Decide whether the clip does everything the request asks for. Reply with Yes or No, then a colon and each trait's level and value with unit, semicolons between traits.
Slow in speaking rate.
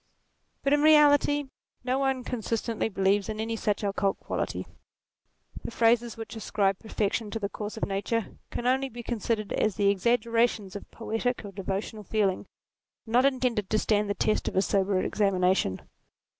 No: average, 165 wpm